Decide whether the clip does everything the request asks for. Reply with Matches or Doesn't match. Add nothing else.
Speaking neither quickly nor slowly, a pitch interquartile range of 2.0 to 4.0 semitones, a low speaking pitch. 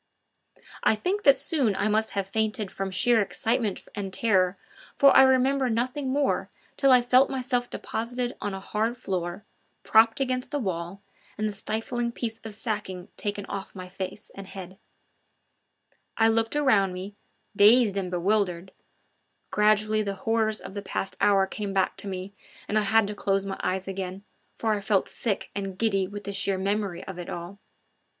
Doesn't match